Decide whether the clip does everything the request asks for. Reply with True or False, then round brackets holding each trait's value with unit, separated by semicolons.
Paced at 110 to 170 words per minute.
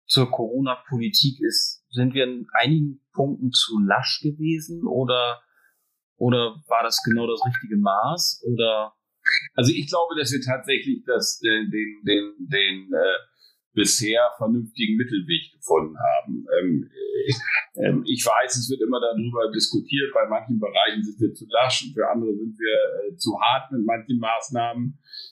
True (155 wpm)